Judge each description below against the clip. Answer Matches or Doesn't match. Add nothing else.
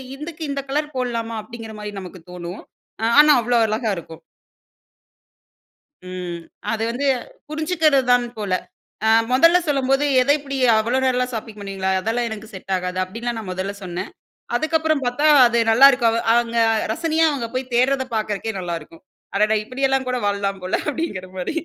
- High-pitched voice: Matches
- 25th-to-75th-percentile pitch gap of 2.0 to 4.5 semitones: Doesn't match